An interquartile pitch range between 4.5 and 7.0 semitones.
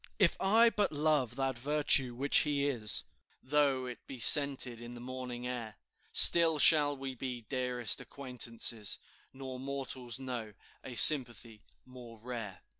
No: average, 2.9 semitones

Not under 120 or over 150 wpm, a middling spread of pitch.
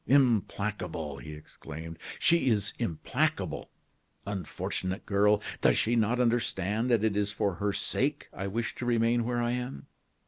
Yes: average, 145 wpm; average, 3.7 semitones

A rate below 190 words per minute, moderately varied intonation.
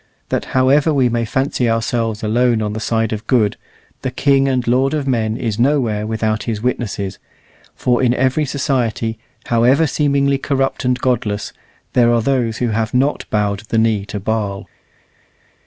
Yes: average, 165 wpm; average, 3.2 semitones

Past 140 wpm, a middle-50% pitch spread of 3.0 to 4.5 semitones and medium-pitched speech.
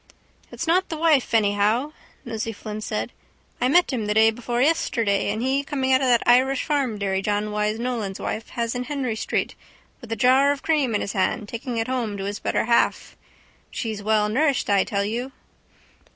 No: average, 195 wpm; average, 3.9 semitones; high, 235 Hz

